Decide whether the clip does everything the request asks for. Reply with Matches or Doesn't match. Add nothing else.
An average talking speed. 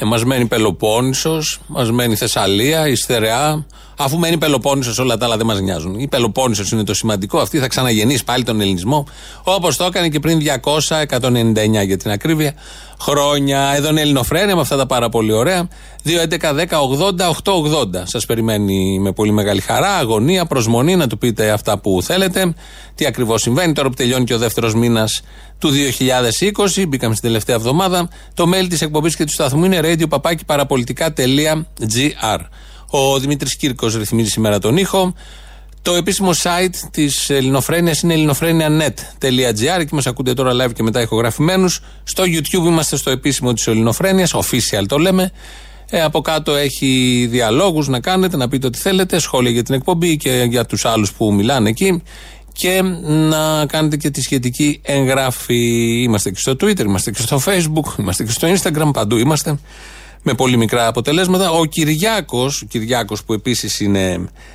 Matches